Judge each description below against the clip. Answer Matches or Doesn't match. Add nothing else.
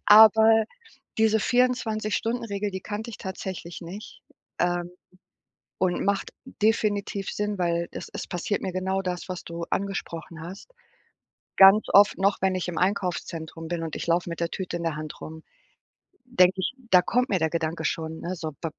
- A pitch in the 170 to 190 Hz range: Matches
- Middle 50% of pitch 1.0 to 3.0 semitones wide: Doesn't match